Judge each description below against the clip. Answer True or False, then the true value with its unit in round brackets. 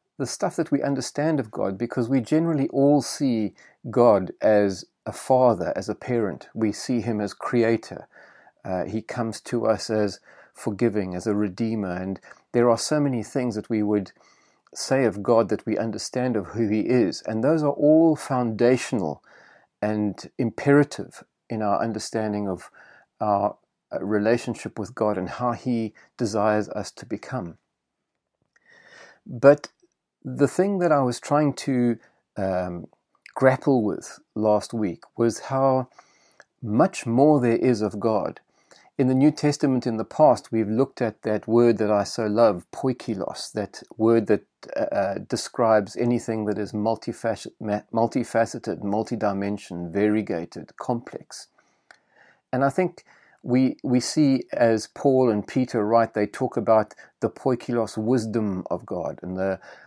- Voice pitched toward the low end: True (115 Hz)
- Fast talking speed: False (145 wpm)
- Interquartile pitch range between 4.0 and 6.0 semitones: False (3.5 semitones)